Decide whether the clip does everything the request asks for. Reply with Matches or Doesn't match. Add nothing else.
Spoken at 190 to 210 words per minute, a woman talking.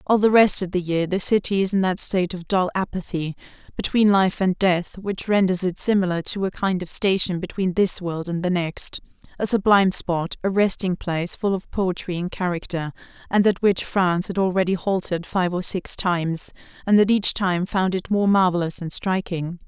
Matches